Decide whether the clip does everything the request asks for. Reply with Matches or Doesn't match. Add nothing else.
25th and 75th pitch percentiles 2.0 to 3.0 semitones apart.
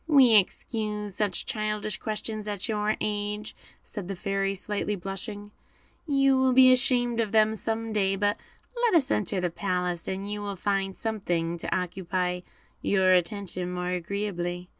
Matches